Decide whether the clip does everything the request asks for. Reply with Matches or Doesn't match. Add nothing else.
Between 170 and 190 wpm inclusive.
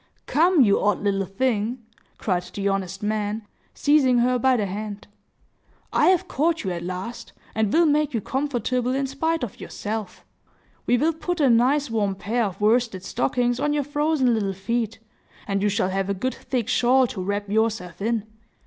Matches